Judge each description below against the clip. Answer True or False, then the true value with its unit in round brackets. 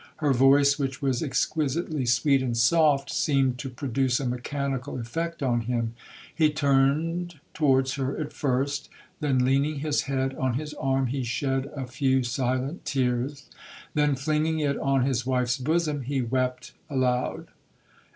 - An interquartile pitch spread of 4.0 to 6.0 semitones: False (2.4 semitones)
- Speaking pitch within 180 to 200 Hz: False (135 Hz)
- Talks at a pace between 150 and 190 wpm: False (140 wpm)